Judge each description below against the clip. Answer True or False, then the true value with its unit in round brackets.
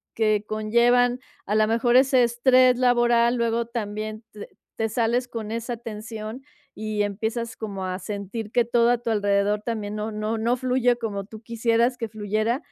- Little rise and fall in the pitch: True (2.1 semitones)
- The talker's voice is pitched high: True (225 Hz)